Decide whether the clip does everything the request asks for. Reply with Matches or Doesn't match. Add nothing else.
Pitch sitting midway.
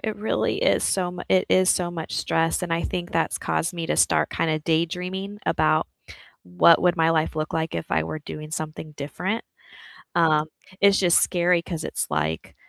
Matches